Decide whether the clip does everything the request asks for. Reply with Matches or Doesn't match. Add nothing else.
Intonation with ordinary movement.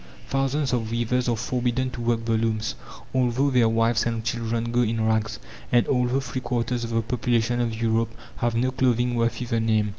Doesn't match